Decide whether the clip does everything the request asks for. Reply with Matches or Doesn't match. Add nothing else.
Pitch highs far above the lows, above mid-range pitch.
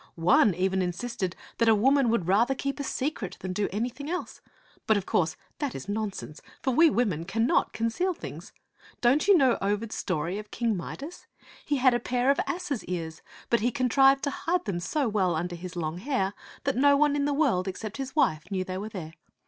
Matches